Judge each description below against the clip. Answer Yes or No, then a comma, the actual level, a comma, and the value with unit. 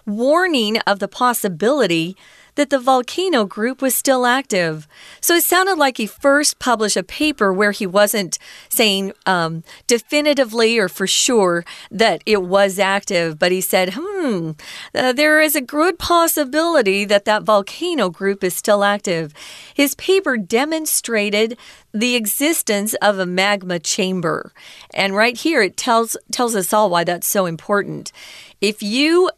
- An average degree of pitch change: No, wide, 6.0 semitones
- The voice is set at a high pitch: Yes, high, 215 Hz